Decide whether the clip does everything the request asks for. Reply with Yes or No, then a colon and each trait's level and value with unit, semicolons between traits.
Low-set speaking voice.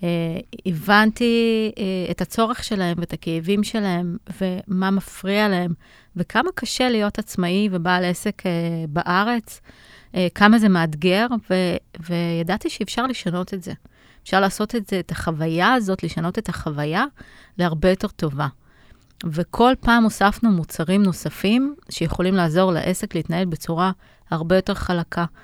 No: medium, 185 Hz